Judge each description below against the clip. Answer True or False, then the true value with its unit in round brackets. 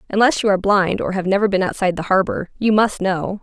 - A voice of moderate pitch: False (195 Hz)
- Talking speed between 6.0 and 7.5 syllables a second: True (6.3 syllables/s)